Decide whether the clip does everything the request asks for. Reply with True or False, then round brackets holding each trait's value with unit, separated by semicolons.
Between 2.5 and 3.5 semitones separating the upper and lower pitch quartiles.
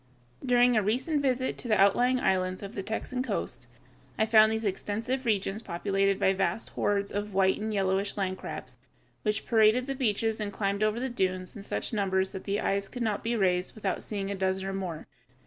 True (2.8 semitones)